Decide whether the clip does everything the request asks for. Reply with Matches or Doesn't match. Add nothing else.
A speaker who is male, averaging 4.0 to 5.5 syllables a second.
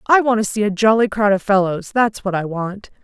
Doesn't match